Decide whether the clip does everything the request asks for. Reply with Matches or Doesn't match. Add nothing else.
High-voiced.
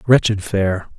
Doesn't match